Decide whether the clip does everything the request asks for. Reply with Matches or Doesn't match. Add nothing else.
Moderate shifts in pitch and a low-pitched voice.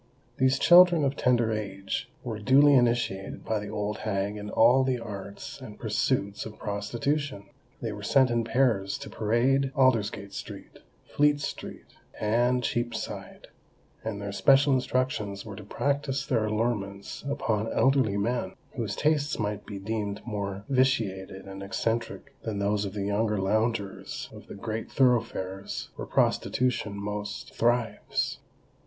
Matches